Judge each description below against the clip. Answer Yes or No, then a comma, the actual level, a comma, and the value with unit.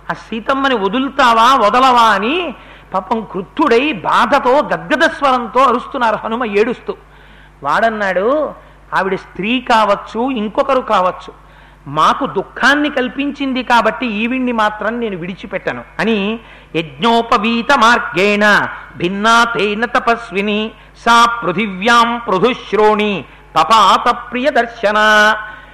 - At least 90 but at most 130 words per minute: No, average, 75 wpm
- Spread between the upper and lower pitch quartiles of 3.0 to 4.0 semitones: Yes, average, 3.4 semitones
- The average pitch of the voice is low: No, high, 225 Hz